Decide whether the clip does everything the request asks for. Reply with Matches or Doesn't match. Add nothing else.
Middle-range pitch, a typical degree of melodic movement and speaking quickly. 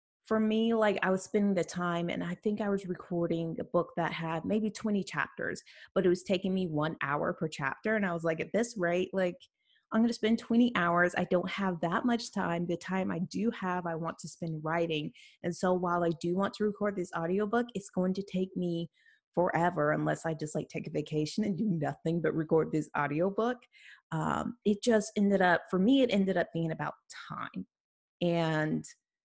Matches